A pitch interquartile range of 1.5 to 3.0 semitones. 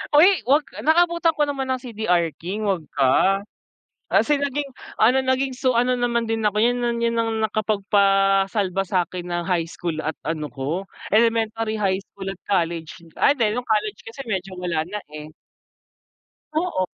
No: average, 4.8 semitones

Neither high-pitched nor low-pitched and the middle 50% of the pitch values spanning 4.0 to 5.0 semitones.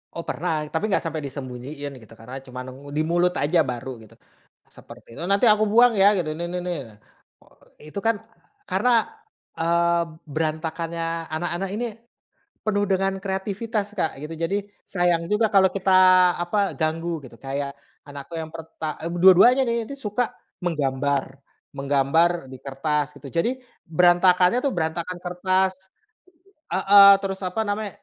Yes: medium, 170 Hz; average, 4.3 semitones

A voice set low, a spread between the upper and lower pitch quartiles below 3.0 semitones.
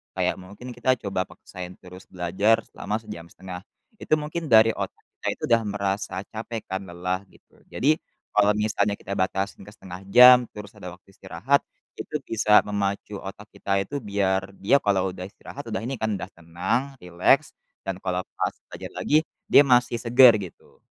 No: low, 100 Hz; average, 3.5 semitones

